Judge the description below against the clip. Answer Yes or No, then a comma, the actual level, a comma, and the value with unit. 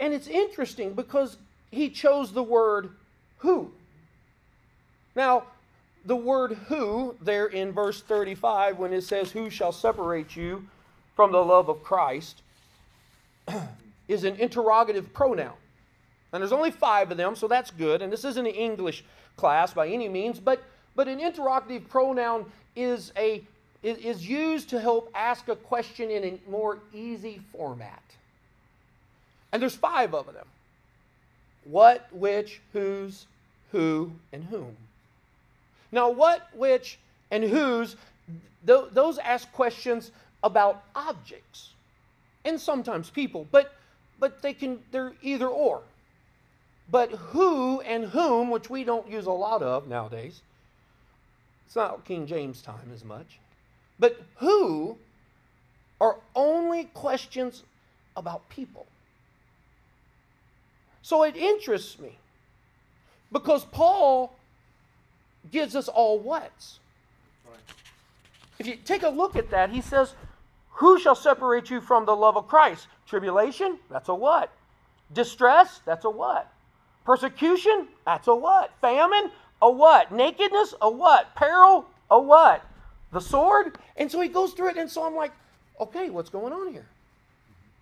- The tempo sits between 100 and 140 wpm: Yes, slow, 135 wpm